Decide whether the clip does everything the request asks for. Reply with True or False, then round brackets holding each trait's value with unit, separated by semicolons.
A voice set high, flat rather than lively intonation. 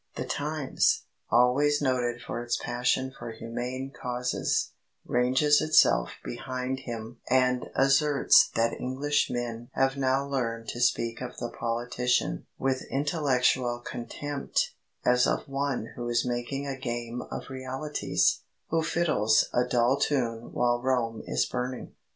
False (125 Hz; 2.2 semitones)